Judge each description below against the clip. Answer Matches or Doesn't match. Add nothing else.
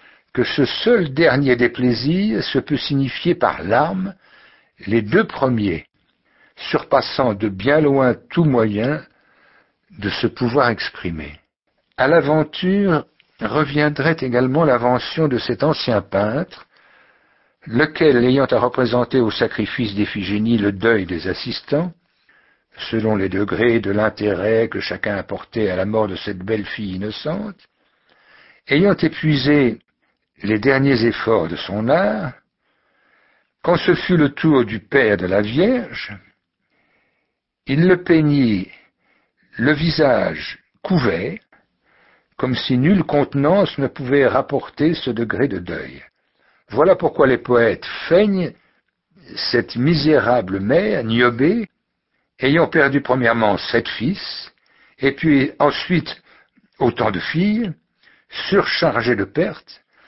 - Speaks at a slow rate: Matches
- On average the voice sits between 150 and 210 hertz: Doesn't match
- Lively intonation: Matches